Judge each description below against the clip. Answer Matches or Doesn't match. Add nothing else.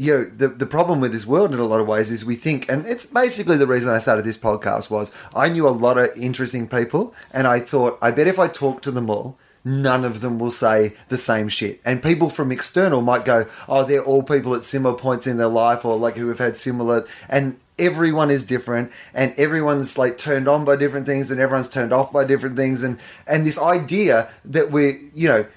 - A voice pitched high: Doesn't match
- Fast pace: Matches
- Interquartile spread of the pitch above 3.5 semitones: Doesn't match